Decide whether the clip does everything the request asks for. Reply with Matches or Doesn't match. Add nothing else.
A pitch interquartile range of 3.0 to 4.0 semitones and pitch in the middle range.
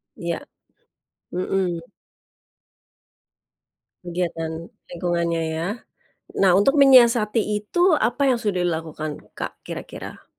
Doesn't match